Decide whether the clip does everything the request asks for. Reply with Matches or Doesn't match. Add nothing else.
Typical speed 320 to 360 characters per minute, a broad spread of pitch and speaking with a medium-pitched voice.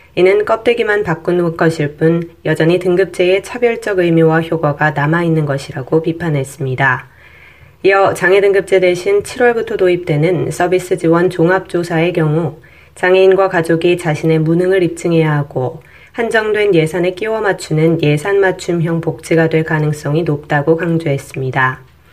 Doesn't match